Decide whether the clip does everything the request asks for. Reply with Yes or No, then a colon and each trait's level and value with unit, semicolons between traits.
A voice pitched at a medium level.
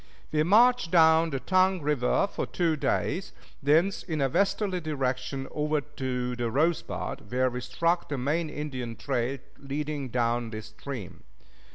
Yes: medium, 145 Hz